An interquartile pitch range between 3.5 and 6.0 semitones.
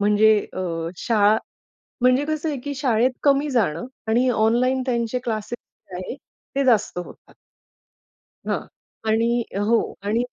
No: average, 3.1 semitones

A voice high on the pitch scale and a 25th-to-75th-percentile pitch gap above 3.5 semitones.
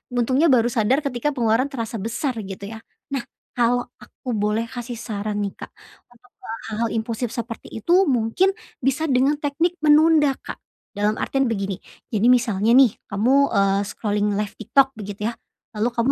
Yes: high, 235 Hz; average, 4.1 semitones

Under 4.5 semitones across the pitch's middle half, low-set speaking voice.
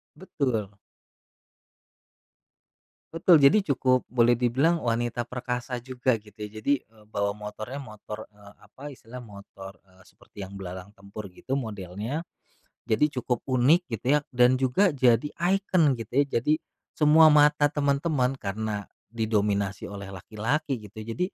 No: average, 5.0 semitones; low, 120 Hz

